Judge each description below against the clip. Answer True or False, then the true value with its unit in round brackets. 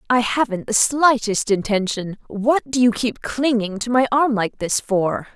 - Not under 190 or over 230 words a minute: False (170 wpm)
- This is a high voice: True (230 Hz)